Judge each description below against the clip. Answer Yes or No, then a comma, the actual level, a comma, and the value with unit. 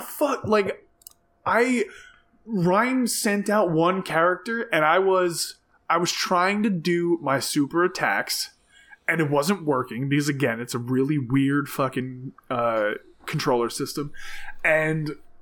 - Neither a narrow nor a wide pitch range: No, wide, 7.2 semitones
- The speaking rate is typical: No, slow, 130 wpm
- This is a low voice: No, medium, 175 Hz